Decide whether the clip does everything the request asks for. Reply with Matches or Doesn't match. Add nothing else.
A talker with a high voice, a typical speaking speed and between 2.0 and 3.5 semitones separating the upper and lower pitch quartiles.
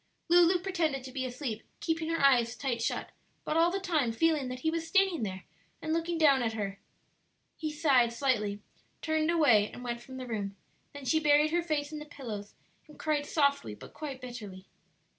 Doesn't match